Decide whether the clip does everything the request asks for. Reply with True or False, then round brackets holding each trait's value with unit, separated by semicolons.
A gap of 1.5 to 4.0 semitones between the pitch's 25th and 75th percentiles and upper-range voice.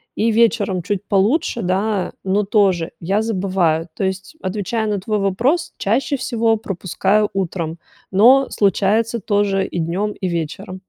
True (2.9 semitones; 200 Hz)